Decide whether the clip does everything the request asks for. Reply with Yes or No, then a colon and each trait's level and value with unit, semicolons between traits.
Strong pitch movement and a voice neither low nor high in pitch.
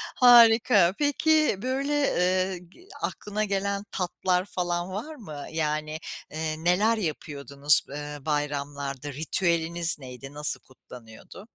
Yes: wide, 5.7 semitones; medium, 175 Hz